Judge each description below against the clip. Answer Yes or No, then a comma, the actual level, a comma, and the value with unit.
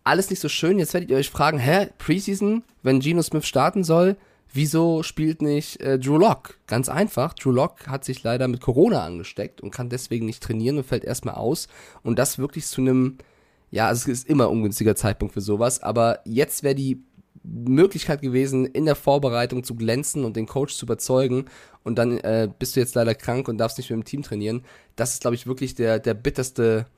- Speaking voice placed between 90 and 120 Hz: No, low, 130 Hz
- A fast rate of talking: Yes, fast, 210 wpm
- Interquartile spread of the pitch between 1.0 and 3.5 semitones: No, average, 4.1 semitones